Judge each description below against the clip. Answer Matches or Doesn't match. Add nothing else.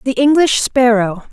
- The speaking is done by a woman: Matches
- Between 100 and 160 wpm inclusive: Matches